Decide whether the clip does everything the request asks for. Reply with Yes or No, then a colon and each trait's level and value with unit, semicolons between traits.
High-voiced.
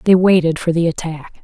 No: medium, 170 Hz